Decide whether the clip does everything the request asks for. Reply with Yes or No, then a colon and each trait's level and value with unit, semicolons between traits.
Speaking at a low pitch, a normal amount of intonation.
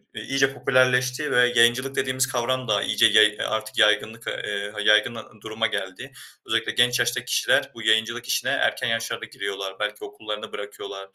Yes: low, 115 Hz; average, 3.0 semitones